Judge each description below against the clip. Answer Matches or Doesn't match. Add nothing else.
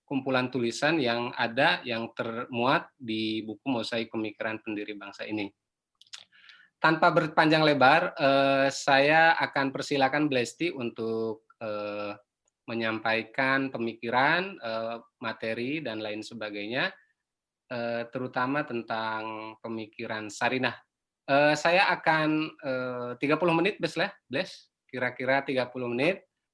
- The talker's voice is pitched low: Matches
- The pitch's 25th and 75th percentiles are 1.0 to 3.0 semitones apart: Doesn't match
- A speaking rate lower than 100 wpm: Matches